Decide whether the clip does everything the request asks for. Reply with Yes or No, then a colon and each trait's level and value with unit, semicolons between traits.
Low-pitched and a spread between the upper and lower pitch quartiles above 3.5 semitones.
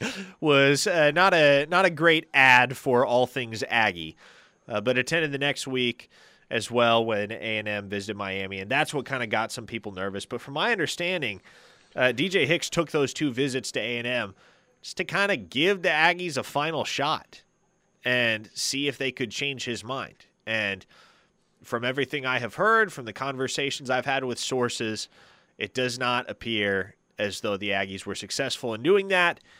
Yes: low, 125 Hz; average, 4.6 semitones